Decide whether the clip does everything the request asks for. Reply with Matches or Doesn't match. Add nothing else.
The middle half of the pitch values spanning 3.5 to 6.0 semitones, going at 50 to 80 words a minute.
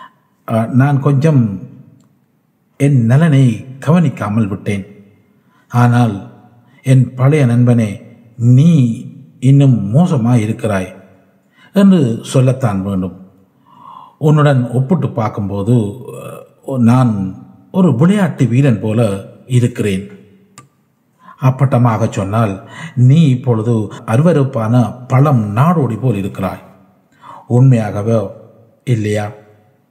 Matches